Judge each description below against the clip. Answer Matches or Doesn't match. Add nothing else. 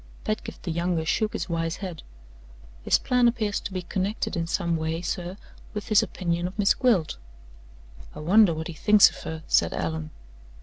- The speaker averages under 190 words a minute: Matches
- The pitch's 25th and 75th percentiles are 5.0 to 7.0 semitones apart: Doesn't match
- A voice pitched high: Doesn't match